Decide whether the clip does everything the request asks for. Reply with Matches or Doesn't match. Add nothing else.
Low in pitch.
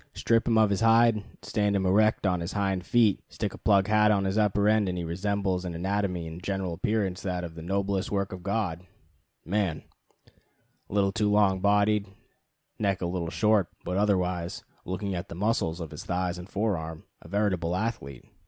Matches